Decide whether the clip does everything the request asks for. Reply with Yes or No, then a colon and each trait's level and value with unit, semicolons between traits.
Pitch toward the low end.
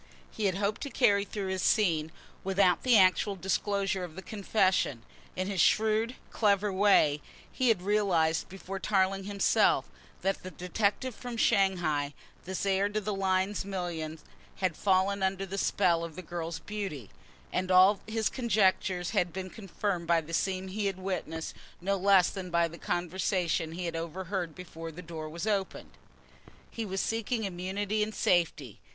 No: high, 190 Hz